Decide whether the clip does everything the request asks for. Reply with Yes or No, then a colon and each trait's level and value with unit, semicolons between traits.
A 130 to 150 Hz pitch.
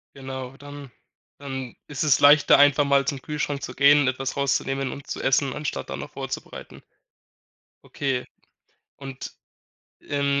Yes: medium, 140 Hz